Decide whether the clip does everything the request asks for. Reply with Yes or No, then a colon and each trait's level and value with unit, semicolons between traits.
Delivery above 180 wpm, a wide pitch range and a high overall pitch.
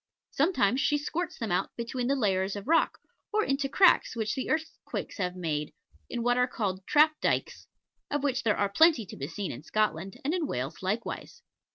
Yes: average, 195 wpm; wide, 7.1 semitones; high, 235 Hz